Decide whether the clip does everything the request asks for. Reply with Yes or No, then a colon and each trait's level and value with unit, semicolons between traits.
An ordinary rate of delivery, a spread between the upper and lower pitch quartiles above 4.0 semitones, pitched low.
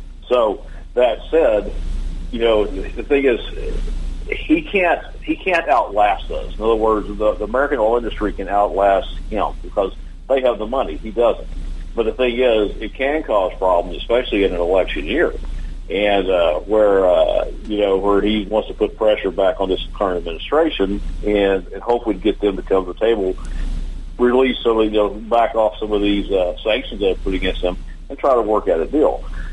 Yes: average, 190 wpm; average, 4.5 semitones; low, 105 Hz